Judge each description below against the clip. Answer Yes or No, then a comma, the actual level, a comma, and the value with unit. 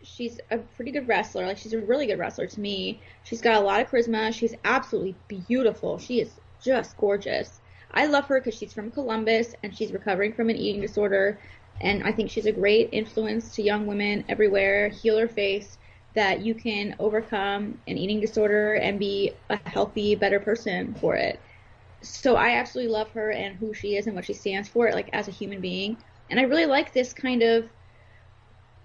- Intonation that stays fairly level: Yes, narrow, 2.1 semitones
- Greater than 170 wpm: Yes, average, 195 wpm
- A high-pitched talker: Yes, high, 215 Hz